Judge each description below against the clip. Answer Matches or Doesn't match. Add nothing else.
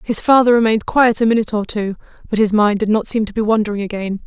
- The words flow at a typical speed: Doesn't match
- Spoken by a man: Doesn't match